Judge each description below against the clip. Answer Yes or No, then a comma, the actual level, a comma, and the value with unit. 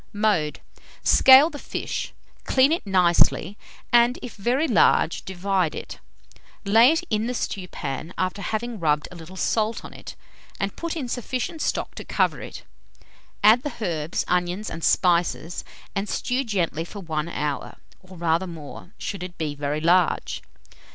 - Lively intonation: Yes, wide, 5.9 semitones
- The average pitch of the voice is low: No, high, 190 Hz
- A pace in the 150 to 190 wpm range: Yes, average, 155 wpm